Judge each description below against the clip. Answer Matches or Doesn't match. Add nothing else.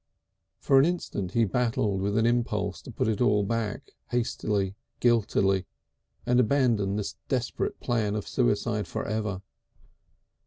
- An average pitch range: Matches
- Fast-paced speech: Doesn't match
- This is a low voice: Matches